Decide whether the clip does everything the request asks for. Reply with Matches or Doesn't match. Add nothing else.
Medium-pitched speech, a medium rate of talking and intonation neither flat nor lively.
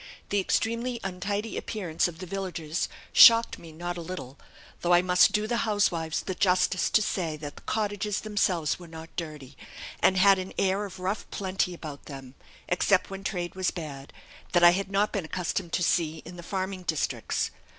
Matches